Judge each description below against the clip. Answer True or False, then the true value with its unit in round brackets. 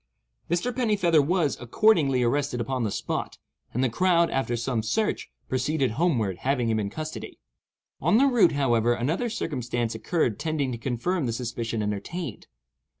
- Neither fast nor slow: True (155 wpm)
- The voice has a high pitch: False (135 Hz)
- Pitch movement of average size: False (6.3 semitones)